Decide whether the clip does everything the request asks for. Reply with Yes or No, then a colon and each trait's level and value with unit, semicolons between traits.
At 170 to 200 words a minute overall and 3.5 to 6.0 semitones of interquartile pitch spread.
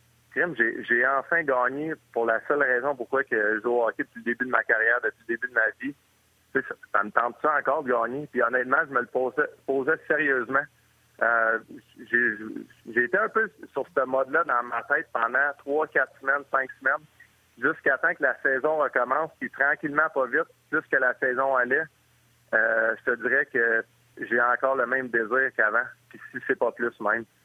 Yes: average, 190 wpm; average, 3.8 semitones